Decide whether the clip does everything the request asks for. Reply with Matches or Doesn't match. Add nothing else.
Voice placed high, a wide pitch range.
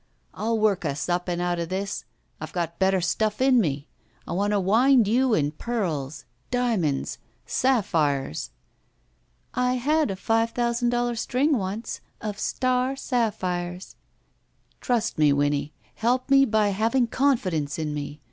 Matches